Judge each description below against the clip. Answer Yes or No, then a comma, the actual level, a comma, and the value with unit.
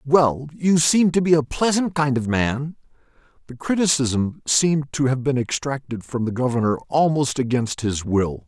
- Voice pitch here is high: No, low, 135 Hz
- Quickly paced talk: No, average, 170 wpm